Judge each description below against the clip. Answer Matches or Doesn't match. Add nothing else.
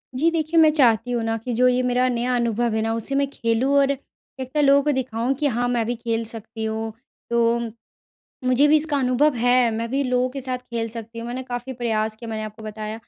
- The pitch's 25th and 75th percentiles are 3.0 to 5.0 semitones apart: Doesn't match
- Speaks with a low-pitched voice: Doesn't match